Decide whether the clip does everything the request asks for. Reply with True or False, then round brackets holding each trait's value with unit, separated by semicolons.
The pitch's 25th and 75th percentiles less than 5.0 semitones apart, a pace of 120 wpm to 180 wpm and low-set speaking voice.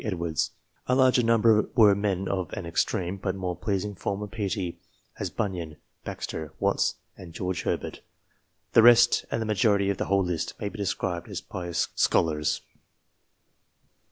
True (3.2 semitones; 155 wpm; 95 Hz)